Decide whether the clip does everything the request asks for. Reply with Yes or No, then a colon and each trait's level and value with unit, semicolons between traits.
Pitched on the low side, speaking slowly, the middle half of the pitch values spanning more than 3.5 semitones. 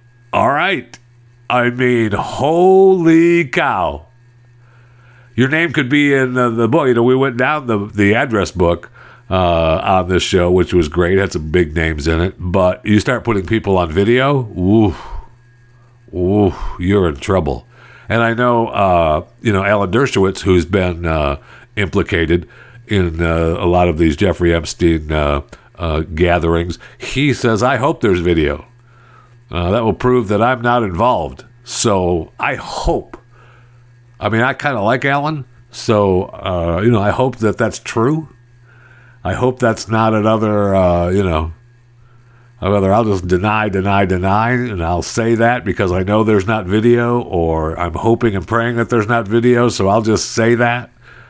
No: low, 110 Hz; average, 165 wpm; average, 4.9 semitones